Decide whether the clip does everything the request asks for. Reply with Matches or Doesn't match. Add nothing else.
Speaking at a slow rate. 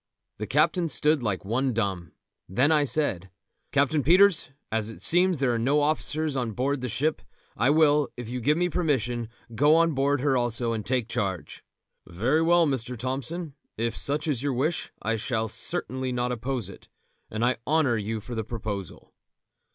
Doesn't match